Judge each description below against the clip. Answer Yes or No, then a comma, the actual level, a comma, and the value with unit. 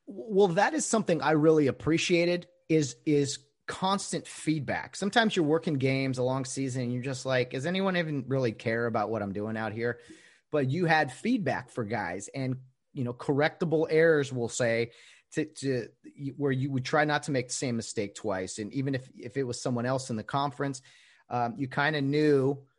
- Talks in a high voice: No, medium, 140 Hz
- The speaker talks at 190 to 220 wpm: Yes, average, 200 wpm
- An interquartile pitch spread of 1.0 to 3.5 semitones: No, average, 3.9 semitones